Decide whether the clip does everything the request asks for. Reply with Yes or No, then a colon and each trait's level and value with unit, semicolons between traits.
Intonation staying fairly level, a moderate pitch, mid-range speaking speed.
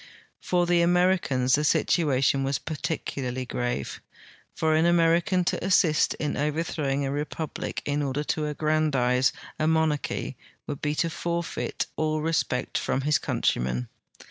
No: average, 3.3 semitones; medium, 150 Hz; average, 145 wpm